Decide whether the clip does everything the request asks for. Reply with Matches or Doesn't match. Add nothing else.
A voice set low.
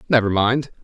Matches